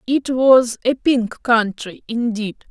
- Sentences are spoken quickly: No, slow, 135 wpm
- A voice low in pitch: No, high, 235 Hz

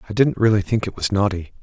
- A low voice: Yes, low, 105 Hz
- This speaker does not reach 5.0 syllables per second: No, 6.7 syllables/s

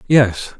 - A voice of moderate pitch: No, low, 120 Hz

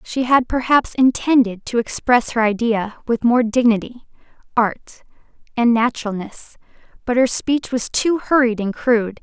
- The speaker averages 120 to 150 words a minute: Yes, average, 145 wpm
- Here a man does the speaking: No, female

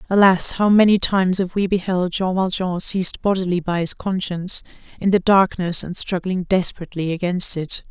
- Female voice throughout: Yes, female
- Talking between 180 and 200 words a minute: No, average, 165 wpm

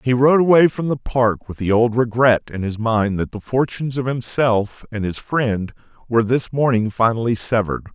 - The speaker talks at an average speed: Yes, average, 195 wpm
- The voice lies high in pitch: No, low, 120 Hz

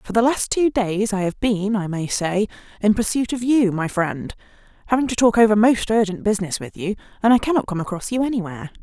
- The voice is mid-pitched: No, high, 210 Hz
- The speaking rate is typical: No, fast, 225 wpm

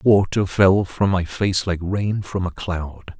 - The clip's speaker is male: Yes, male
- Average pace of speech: Yes, average, 190 wpm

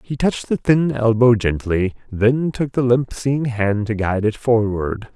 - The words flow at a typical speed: Yes, average, 185 wpm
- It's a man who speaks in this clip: Yes, male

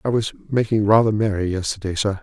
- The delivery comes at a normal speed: Yes, average, 190 wpm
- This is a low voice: Yes, low, 105 Hz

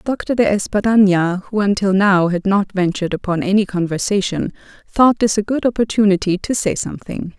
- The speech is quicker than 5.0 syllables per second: Yes, 5.6 syllables/s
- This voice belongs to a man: No, female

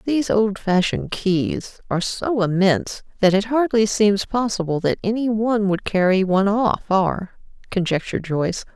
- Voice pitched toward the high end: Yes, high, 200 Hz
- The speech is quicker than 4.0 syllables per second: Yes, 5.0 syllables/s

